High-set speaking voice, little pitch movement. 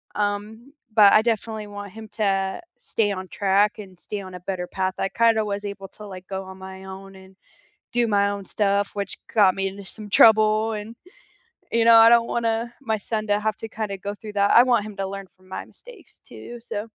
Yes: high, 205 Hz; narrow, 2.3 semitones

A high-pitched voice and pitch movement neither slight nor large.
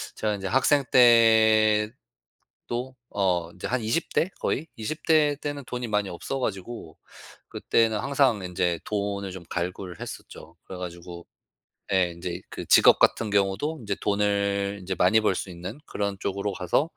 No: low, 100 Hz; average, 4.3 semitones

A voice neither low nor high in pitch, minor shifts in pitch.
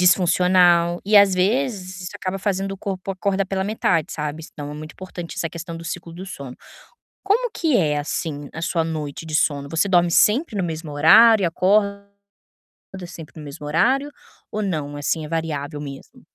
No: medium, 175 Hz; average, 4.0 semitones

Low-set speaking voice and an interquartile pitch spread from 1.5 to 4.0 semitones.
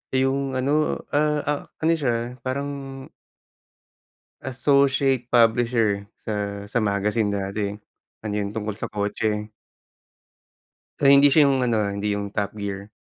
No: low, 115 Hz; average, 4.9 semitones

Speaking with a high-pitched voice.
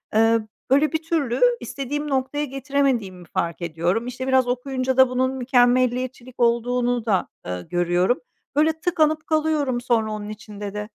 Yes: very high, 250 Hz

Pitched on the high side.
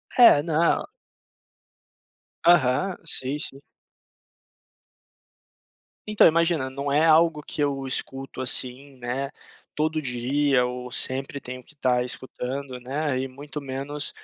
No: medium, 140 Hz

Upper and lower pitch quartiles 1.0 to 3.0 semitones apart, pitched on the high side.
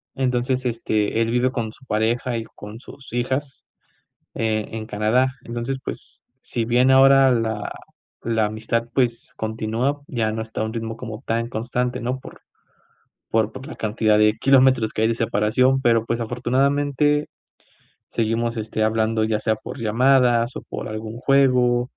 No: narrow, 2.5 semitones; low, 115 Hz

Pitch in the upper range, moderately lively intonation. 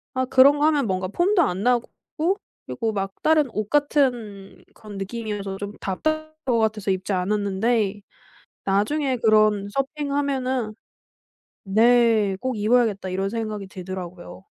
Yes: high, 215 Hz; average, 4.8 semitones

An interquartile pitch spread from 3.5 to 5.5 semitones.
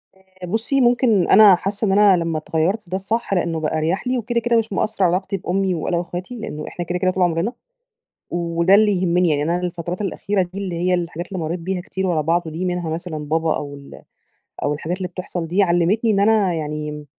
No: average, 3.0 semitones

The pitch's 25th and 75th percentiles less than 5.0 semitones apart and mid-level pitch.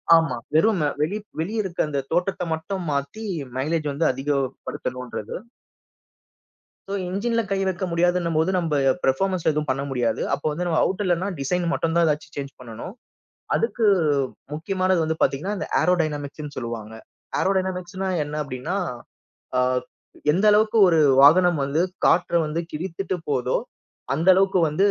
Yes: average, 4.6 semitones; medium, 165 Hz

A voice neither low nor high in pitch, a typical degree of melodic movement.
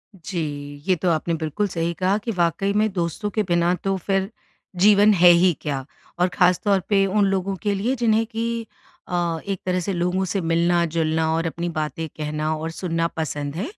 Yes: medium, 175 Hz; average, 3.3 semitones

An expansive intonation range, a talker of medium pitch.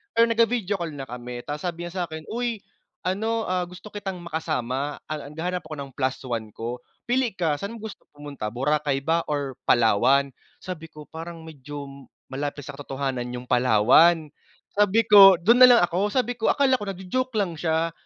Yes: wide, 6.3 semitones; medium, 160 Hz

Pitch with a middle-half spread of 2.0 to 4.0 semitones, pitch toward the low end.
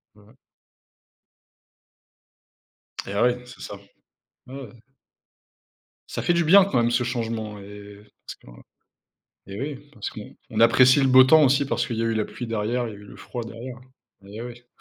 Yes: average, 3.0 semitones; low, 120 Hz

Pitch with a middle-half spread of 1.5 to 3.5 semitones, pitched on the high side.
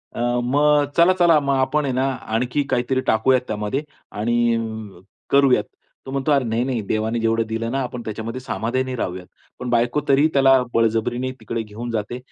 No: average, 3.0 semitones; low, 120 Hz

